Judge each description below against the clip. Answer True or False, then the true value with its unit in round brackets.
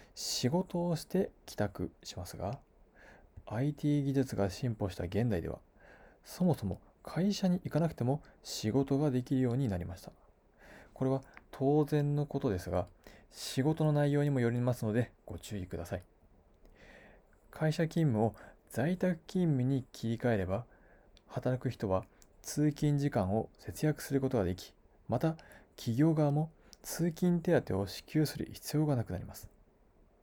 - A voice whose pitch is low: True (130 Hz)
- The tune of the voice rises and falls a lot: True (6.8 semitones)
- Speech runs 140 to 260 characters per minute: False (280 characters per minute)